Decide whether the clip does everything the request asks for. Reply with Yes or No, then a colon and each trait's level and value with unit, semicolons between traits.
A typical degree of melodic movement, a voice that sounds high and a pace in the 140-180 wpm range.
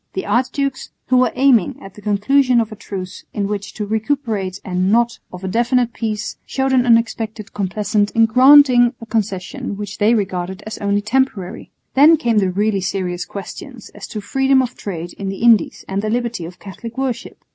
No: average, 3.8 semitones; high, 215 Hz; average, 190 wpm